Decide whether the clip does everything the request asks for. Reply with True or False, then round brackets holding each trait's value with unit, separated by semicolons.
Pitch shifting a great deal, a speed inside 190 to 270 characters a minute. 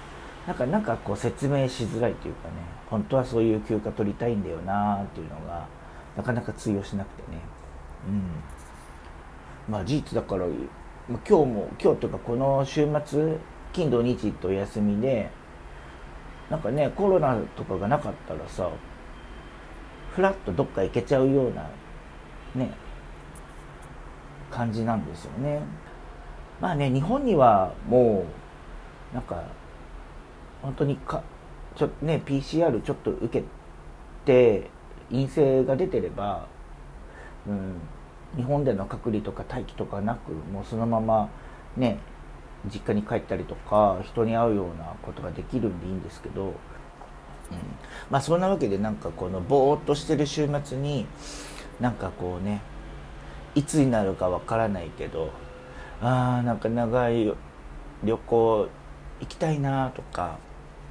True (7.6 semitones; 265 characters per minute)